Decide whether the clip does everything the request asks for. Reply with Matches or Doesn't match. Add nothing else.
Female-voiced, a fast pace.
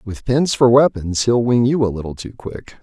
Doesn't match